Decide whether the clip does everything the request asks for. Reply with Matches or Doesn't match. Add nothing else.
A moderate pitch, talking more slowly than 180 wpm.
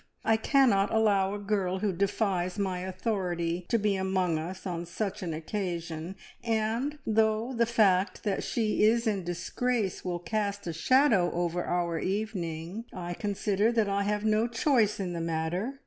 Doesn't match